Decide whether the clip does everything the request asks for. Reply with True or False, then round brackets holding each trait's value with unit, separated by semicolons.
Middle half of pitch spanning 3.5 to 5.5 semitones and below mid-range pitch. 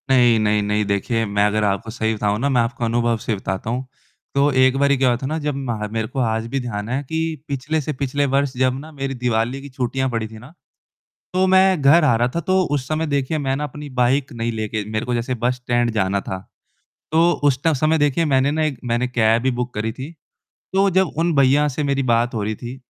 True (3.8 semitones; 130 Hz)